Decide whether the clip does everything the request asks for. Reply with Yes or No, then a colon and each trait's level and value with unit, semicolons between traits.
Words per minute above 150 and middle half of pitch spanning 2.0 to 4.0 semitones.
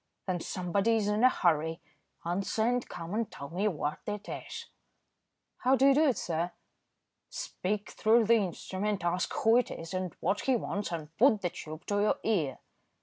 No: average, 185 wpm; average, 4.5 semitones